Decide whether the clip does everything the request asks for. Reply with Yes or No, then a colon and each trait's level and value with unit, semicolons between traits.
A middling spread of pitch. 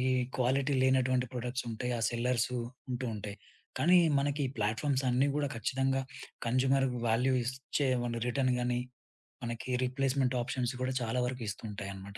No: narrow, 2.2 semitones